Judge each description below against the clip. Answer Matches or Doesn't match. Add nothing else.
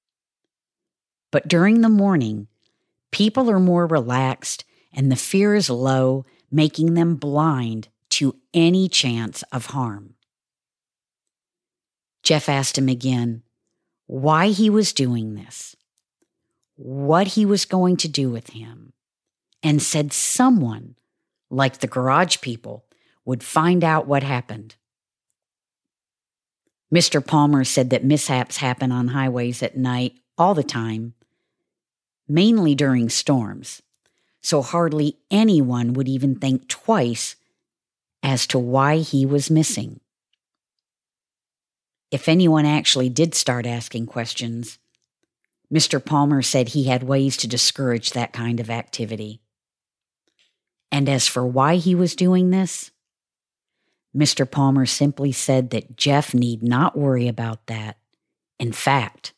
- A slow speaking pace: Matches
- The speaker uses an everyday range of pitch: Matches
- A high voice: Doesn't match